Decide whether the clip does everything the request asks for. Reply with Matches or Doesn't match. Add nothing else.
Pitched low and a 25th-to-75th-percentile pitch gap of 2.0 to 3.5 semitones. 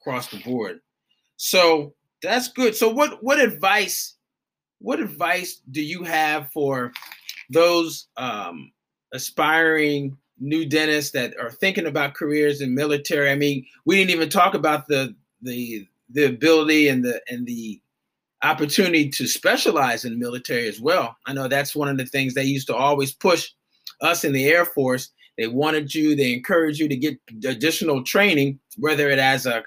Doesn't match